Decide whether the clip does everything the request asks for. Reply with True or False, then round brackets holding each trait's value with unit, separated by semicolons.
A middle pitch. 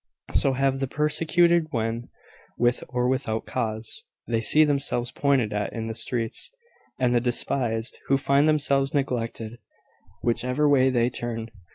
False (125 Hz)